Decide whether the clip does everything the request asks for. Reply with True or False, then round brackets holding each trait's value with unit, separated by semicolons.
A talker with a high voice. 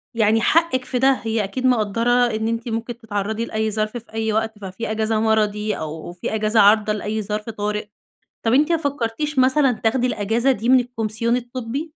True (225 Hz)